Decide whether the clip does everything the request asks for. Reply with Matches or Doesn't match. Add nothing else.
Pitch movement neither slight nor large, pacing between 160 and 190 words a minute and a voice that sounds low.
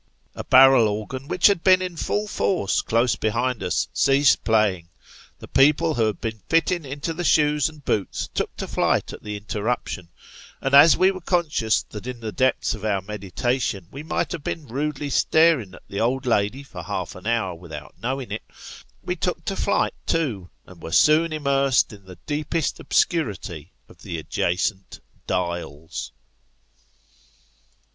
Doesn't match